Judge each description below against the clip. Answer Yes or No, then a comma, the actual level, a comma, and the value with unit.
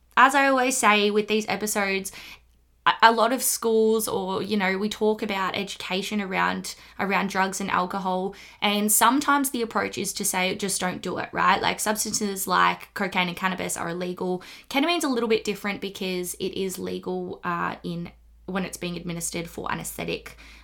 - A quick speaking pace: No, average, 175 wpm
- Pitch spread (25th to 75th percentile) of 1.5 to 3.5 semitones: Yes, average, 2.9 semitones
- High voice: Yes, high, 195 Hz